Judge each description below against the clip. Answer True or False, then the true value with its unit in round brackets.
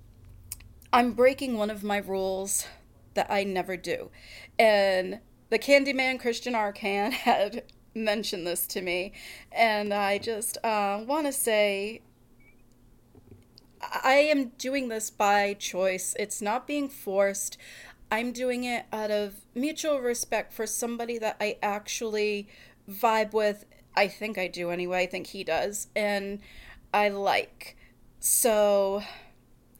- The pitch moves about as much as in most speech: True (3.4 semitones)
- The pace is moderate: False (130 wpm)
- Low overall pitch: False (210 Hz)